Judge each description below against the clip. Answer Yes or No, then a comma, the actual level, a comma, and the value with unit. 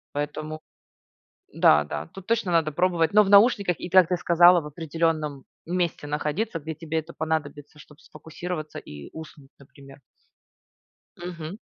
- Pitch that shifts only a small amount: No, average, 3.0 semitones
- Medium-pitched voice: Yes, medium, 160 Hz